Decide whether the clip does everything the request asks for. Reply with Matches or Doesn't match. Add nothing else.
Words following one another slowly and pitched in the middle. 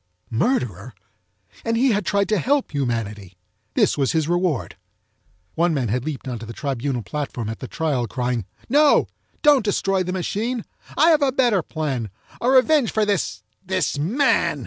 Doesn't match